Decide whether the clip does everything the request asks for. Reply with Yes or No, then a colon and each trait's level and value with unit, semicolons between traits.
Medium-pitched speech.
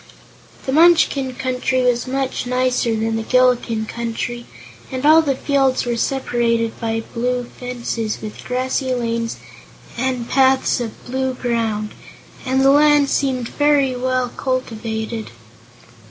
No: very high, 250 Hz